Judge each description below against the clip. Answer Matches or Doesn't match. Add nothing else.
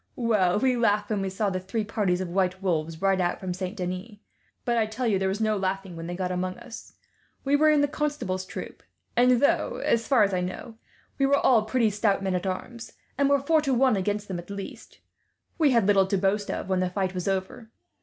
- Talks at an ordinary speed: Doesn't match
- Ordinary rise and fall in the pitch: Matches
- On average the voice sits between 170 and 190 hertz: Doesn't match